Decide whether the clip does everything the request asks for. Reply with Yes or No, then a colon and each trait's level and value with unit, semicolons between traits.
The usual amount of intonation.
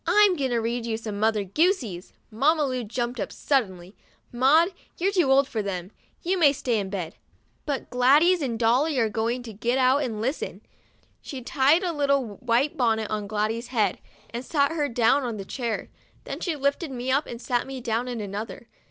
Yes: average, 4.1 semitones